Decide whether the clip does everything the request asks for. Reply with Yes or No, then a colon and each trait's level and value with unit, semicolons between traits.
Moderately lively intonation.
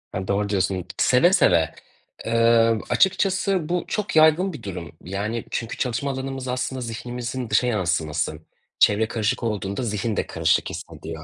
Yes: average, 4.8 semitones